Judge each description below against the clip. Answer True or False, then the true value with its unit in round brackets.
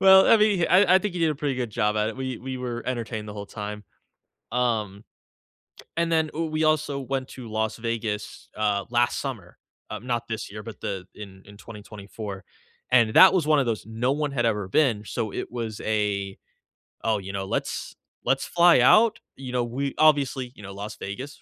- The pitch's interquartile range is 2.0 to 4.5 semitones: False (4.9 semitones)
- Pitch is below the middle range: True (120 Hz)